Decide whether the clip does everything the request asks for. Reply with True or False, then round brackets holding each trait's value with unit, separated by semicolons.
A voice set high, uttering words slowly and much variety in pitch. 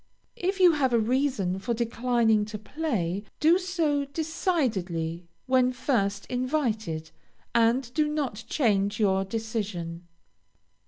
True (235 Hz; 115 wpm; 6.2 semitones)